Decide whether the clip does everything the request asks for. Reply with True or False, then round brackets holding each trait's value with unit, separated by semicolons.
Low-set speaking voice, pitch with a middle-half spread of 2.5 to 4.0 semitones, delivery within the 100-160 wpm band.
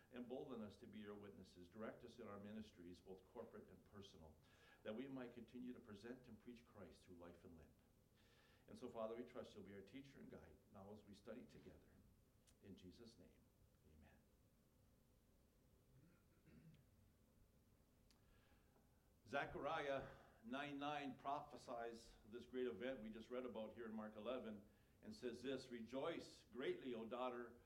True (115 Hz; 3.6 semitones; 150 wpm)